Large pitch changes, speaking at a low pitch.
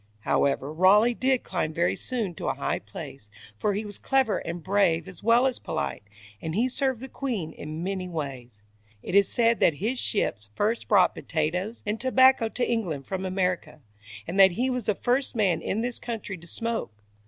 No: wide, 6.2 semitones; high, 200 Hz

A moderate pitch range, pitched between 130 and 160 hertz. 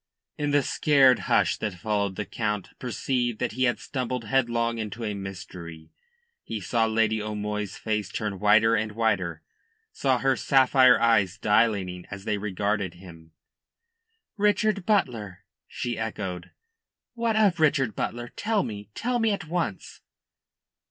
No: average, 4.3 semitones; low, 110 Hz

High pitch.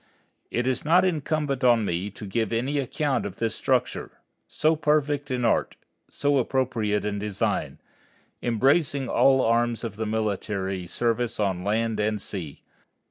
No: low, 115 Hz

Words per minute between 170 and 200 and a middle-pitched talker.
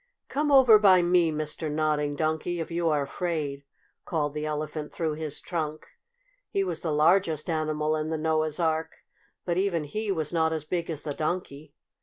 Yes: average, 180 wpm; medium, 160 Hz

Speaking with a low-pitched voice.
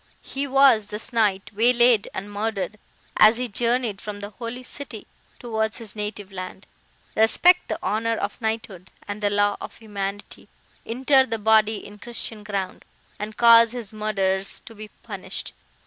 No: high, 215 Hz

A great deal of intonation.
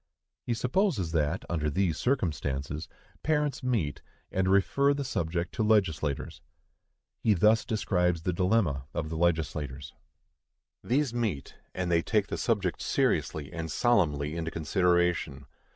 Yes: wide, 6.2 semitones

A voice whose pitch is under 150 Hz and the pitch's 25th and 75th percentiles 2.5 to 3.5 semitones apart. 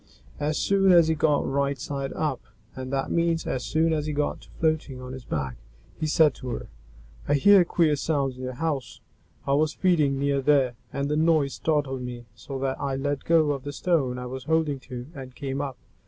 Yes: medium, 140 Hz; average, 3.0 semitones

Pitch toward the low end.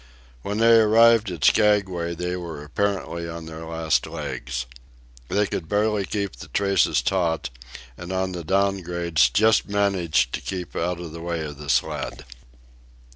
Yes: very low, 90 Hz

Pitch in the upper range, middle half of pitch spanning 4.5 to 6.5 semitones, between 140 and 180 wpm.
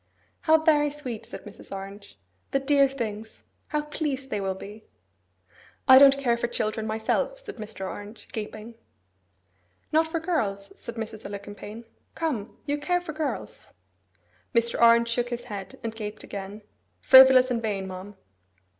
Yes: high, 235 Hz; average, 5.0 semitones; average, 150 wpm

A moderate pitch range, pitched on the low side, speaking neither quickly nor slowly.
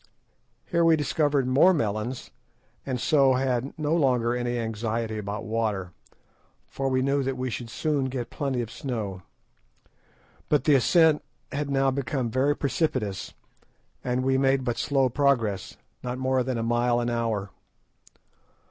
Yes: average, 3.0 semitones; low, 130 Hz; average, 150 wpm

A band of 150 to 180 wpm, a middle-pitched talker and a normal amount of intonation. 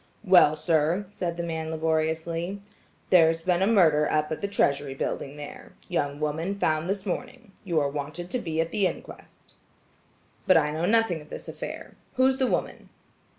Yes: average, 170 wpm; medium, 165 Hz; average, 3.5 semitones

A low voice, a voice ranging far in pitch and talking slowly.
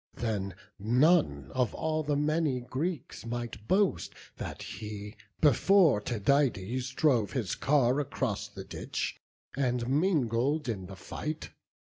Yes: low, 125 Hz; wide, 5.7 semitones; slow, 120 wpm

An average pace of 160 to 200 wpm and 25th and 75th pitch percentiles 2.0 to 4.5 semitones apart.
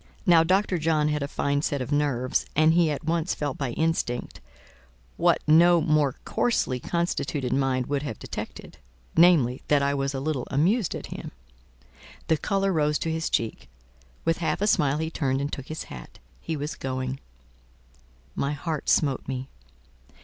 Yes: average, 165 wpm; average, 3.3 semitones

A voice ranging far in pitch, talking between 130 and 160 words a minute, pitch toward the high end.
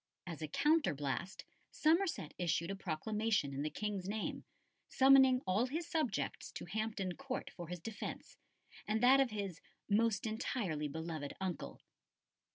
Yes: wide, 6.7 semitones; average, 140 wpm; high, 205 Hz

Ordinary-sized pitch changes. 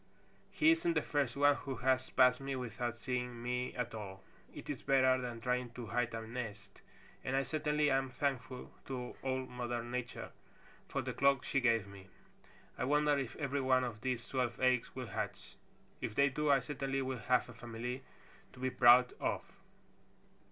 No: narrow, 2.0 semitones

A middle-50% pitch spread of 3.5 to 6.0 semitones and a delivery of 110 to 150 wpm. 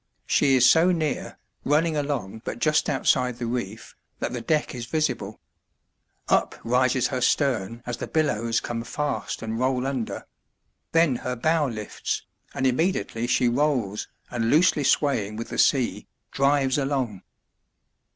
Yes: average, 3.9 semitones; average, 145 wpm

